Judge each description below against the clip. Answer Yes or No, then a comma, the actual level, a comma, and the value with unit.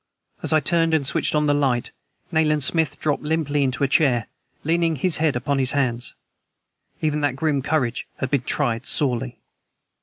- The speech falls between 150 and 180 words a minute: Yes, average, 175 wpm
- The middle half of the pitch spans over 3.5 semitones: No, average, 3.1 semitones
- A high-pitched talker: No, medium, 145 Hz